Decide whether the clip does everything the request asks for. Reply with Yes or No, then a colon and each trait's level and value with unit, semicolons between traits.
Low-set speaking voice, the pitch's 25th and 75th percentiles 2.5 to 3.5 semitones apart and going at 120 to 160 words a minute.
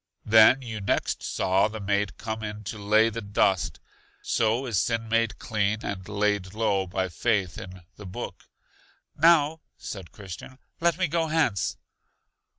Yes: low, 105 Hz; average, 2.8 semitones; average, 155 wpm